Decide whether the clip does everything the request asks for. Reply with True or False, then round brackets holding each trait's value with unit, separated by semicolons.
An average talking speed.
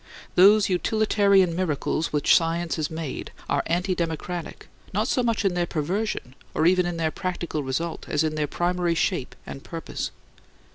True (160 wpm)